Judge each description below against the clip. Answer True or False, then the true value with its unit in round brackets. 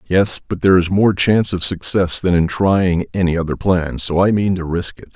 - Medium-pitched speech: False (90 Hz)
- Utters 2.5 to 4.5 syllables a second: False (5.2 syllables/s)